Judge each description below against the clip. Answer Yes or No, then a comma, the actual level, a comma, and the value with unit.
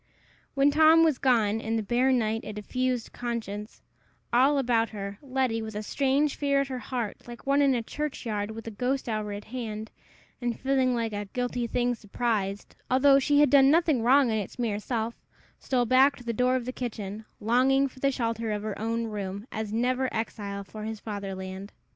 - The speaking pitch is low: No, high, 235 Hz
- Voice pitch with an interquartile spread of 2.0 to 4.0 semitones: Yes, average, 3.4 semitones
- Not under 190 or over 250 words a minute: Yes, average, 195 wpm